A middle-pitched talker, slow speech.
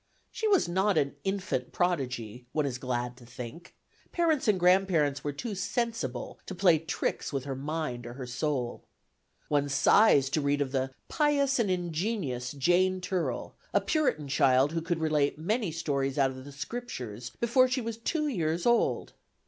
No: medium, 155 Hz; average, 170 wpm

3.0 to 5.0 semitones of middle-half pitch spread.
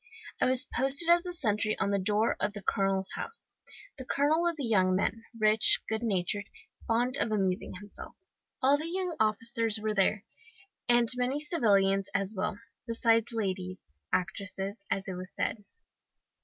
Yes: average, 4.1 semitones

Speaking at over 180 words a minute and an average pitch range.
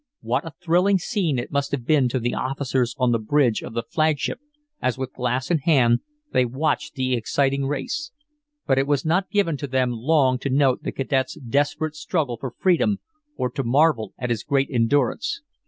Yes: average, 190 wpm; average, 3.7 semitones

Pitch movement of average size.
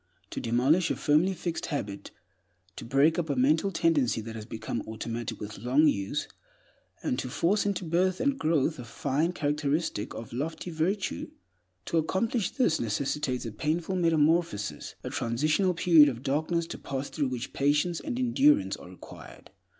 No: wide, 5.8 semitones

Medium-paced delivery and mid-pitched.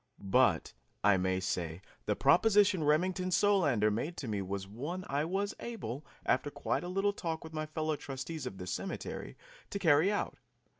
Yes: average, 170 wpm; medium, 155 Hz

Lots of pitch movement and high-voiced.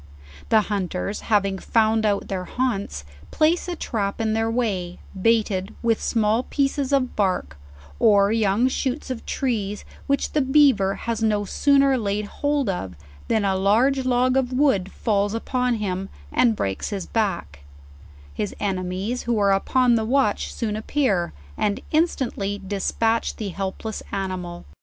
No: average, 4.3 semitones; high, 215 Hz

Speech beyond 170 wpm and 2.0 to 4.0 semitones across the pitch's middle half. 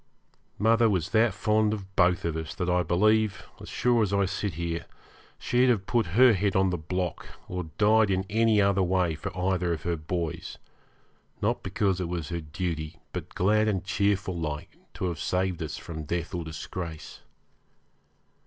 Yes: average, 180 wpm; average, 3.5 semitones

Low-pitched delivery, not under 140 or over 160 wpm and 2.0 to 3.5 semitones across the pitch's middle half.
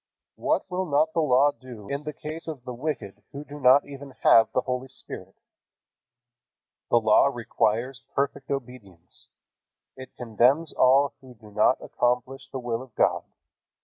Yes: low, 130 Hz; average, 155 wpm; average, 3.1 semitones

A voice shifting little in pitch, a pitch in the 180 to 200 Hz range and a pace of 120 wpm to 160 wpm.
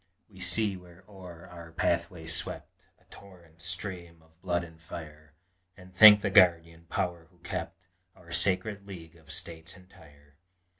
No: narrow, 2.0 semitones; very low, 85 Hz; average, 150 wpm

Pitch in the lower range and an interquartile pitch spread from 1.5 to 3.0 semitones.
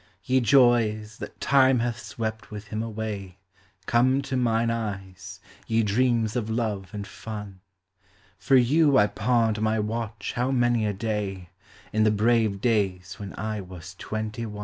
Yes: low, 110 Hz; narrow, 2.5 semitones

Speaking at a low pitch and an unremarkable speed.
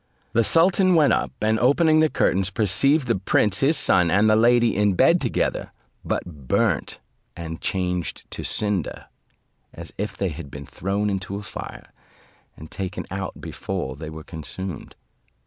Yes: low, 100 Hz; average, 160 wpm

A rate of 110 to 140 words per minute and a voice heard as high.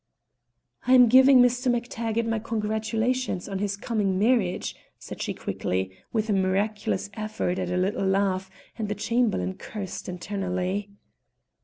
Yes: slow, 135 wpm; high, 210 Hz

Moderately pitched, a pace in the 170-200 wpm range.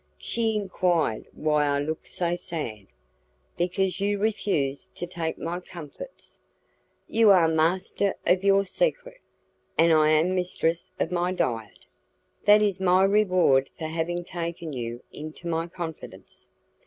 No: medium, 175 Hz; slow, 135 wpm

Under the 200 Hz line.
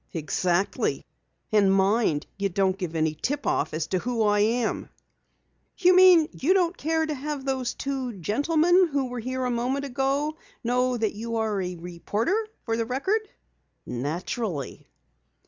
No: high, 240 Hz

